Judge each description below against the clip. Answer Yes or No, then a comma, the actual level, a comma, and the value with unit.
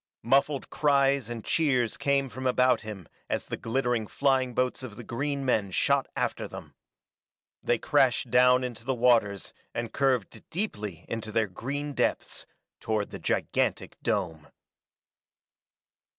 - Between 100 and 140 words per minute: Yes, slow, 135 wpm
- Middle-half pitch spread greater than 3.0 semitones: Yes, average, 3.6 semitones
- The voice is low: Yes, low, 125 Hz